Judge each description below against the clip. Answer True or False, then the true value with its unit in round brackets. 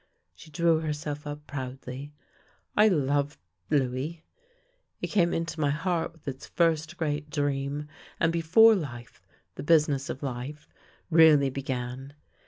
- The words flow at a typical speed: True (155 wpm)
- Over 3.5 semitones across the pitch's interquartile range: False (3.0 semitones)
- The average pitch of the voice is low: False (150 Hz)